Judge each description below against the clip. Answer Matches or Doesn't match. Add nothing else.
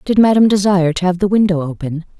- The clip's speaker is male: Doesn't match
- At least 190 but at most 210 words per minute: Doesn't match